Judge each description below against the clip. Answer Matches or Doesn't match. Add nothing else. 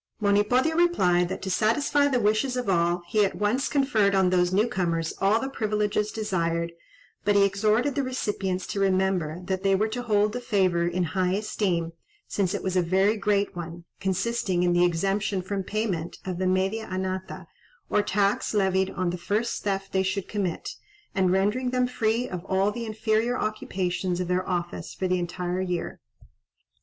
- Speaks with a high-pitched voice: Matches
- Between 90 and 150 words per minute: Doesn't match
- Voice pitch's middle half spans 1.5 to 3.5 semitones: Matches